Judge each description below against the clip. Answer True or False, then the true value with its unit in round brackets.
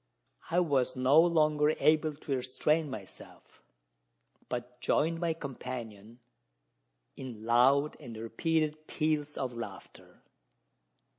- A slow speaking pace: True (100 wpm)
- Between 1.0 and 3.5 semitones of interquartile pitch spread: False (4.1 semitones)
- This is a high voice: False (140 Hz)